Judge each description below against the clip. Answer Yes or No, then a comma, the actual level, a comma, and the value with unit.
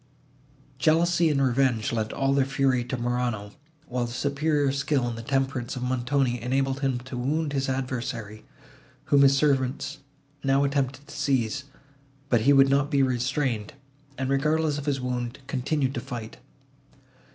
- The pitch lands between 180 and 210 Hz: No, low, 135 Hz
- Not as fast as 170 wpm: Yes, average, 155 wpm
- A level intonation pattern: Yes, narrow, 2.3 semitones